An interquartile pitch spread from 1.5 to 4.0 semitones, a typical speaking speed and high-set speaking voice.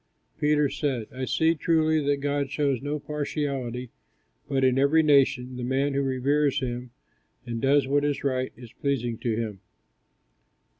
No: narrow, 2.4 semitones; average, 155 wpm; medium, 140 Hz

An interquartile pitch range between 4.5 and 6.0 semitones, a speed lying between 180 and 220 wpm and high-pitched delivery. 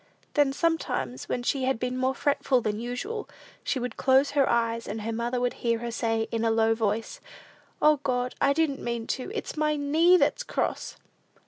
No: average, 3.9 semitones; average, 195 wpm; very high, 250 Hz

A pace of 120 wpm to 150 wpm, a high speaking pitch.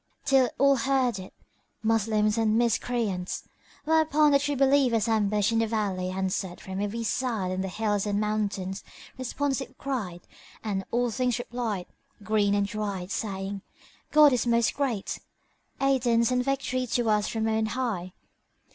Yes: average, 145 wpm; high, 225 Hz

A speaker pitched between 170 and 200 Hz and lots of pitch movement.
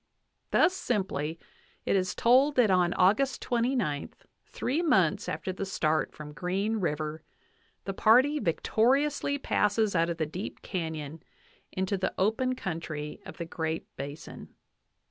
Yes: high, 190 Hz; wide, 6.5 semitones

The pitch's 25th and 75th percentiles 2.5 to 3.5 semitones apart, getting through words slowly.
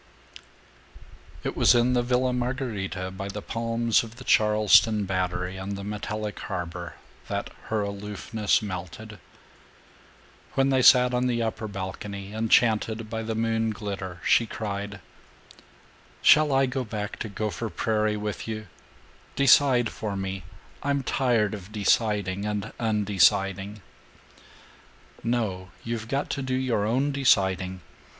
Yes: average, 3.0 semitones; slow, 130 wpm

